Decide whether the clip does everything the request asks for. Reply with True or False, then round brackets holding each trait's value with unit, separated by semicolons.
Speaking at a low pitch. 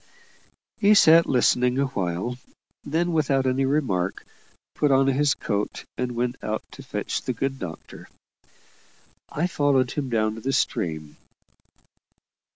True (130 Hz)